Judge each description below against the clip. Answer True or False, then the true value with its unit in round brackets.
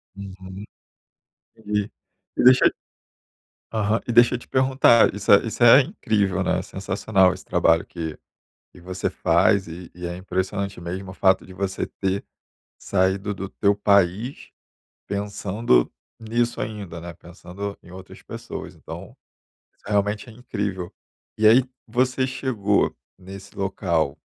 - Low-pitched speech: True (100 Hz)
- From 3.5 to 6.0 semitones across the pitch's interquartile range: False (2.9 semitones)